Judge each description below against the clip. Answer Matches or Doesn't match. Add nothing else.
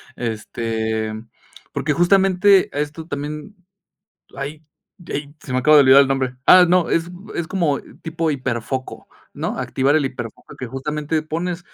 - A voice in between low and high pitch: Matches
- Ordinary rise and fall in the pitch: Matches